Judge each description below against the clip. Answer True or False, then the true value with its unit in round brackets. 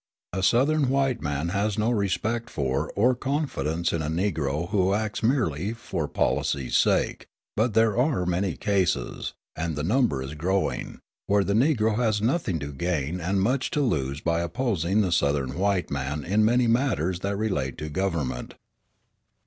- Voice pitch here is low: True (95 Hz)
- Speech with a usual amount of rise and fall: False (6.3 semitones)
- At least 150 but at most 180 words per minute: True (165 wpm)